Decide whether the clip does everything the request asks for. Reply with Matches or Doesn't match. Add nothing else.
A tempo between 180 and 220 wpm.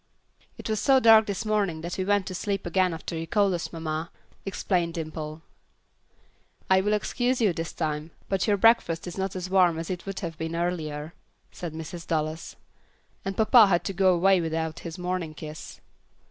Matches